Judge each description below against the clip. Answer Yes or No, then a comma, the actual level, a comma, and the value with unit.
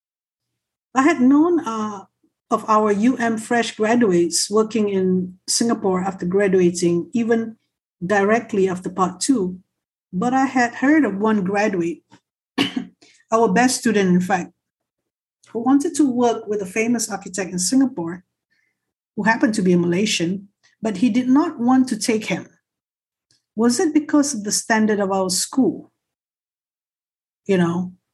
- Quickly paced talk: No, average, 140 wpm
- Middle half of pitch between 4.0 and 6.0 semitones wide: Yes, average, 4.3 semitones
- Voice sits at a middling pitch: No, high, 220 Hz